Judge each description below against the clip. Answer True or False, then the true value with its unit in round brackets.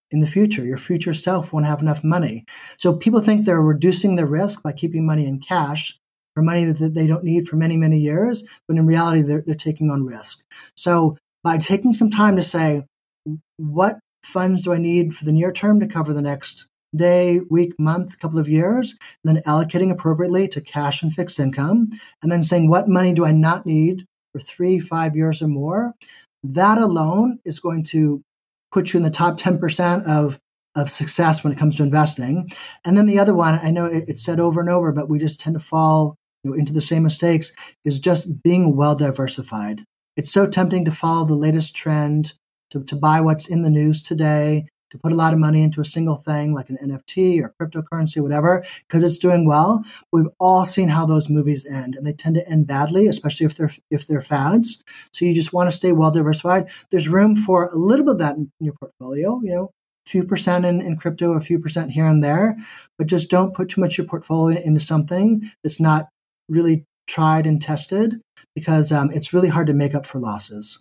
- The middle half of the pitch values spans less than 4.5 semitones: True (2.9 semitones)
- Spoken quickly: True (215 wpm)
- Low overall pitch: False (160 Hz)